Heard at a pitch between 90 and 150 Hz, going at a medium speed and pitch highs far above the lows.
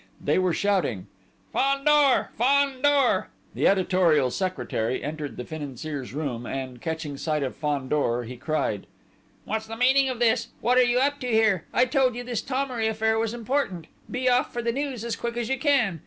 No: high, 220 Hz; average, 180 wpm; wide, 8.8 semitones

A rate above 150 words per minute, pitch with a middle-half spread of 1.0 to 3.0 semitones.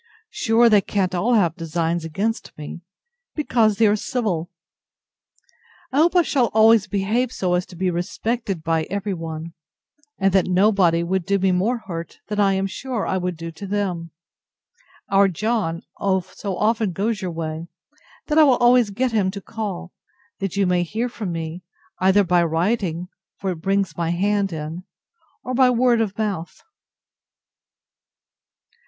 No: average, 160 wpm; average, 4.2 semitones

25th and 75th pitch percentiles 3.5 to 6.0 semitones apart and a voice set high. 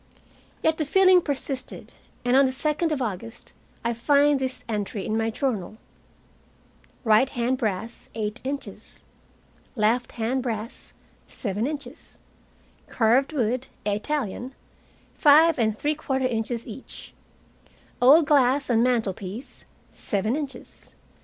Yes: average, 4.1 semitones; very high, 250 Hz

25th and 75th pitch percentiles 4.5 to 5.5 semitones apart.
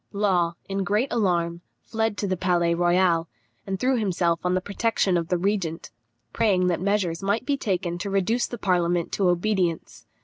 No: average, 2.9 semitones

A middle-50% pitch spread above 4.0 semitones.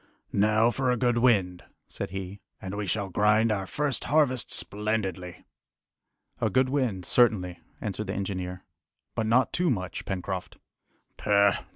Yes: average, 4.4 semitones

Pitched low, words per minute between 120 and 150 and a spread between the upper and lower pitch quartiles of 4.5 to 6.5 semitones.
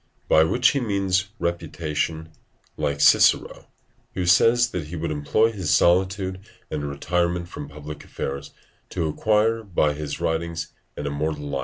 No: very low, 85 Hz; average, 145 wpm; average, 4.0 semitones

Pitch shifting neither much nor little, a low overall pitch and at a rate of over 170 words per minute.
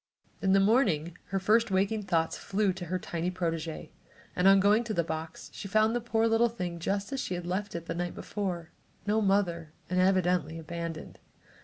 No: average, 3.5 semitones; medium, 185 Hz; average, 195 wpm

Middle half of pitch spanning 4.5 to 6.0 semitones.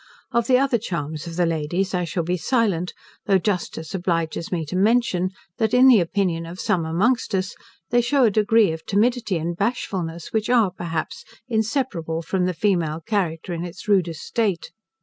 Yes: average, 4.8 semitones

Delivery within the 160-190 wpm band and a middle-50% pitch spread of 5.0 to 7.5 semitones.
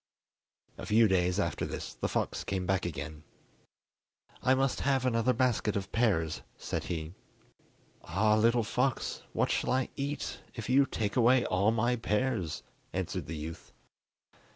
No: average, 150 wpm; wide, 5.6 semitones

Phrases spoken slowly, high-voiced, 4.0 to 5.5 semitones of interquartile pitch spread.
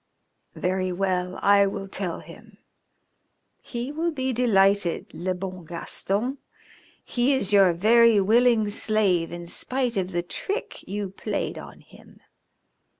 Yes: slow, 125 wpm; high, 200 Hz; average, 4.3 semitones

